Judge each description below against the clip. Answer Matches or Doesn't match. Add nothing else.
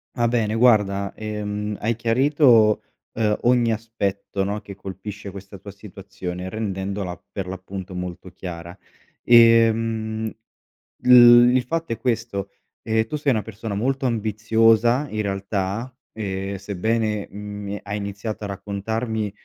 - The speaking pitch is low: Matches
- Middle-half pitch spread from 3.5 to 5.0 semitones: Doesn't match